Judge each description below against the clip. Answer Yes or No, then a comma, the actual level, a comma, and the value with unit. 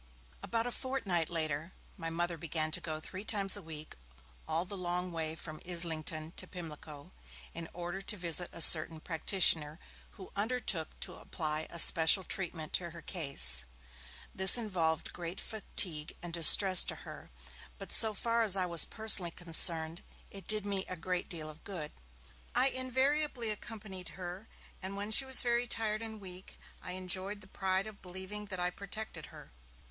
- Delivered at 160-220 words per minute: Yes, average, 170 wpm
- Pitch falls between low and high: Yes, medium, 180 Hz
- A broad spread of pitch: No, average, 4.0 semitones